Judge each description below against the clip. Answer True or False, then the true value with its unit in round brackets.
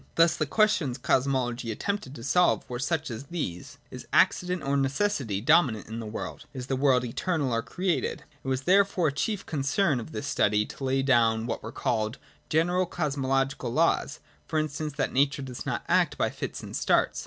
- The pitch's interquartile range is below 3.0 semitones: False (4.9 semitones)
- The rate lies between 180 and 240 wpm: True (190 wpm)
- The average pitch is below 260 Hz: True (140 Hz)